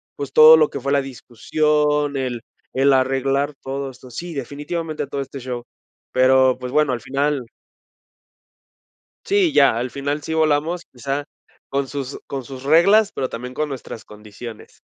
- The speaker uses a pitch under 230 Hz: Yes, medium, 140 Hz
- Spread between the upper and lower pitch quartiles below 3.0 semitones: Yes, narrow, 2.4 semitones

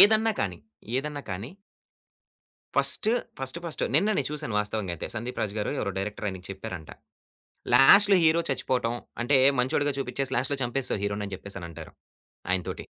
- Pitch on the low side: Yes, low, 125 Hz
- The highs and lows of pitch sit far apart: Yes, wide, 6.3 semitones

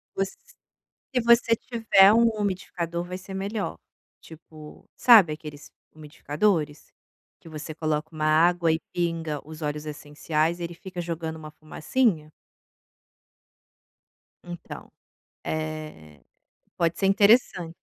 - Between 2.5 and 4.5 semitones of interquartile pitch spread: Yes, average, 3.9 semitones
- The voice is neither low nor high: Yes, medium, 165 Hz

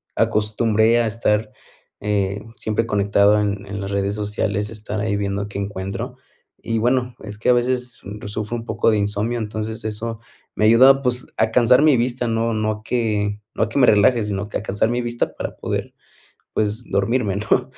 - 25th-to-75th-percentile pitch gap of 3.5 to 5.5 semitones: No, narrow, 2.4 semitones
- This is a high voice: No, low, 110 Hz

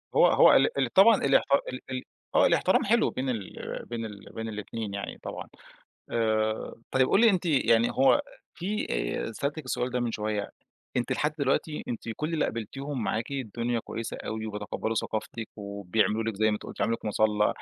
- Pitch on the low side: Yes, low, 115 Hz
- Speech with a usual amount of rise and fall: Yes, average, 3.9 semitones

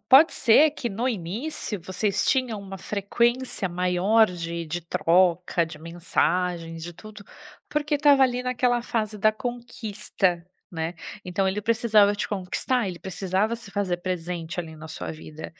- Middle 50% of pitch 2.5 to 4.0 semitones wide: No, average, 5.0 semitones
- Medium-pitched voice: No, high, 195 Hz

